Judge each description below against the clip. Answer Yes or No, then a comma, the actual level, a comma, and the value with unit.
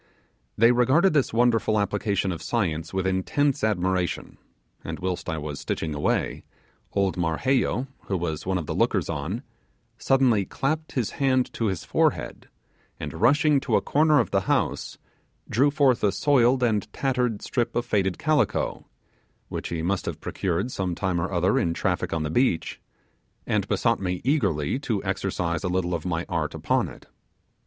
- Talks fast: No, average, 165 wpm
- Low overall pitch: Yes, low, 100 Hz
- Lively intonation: Yes, wide, 6.3 semitones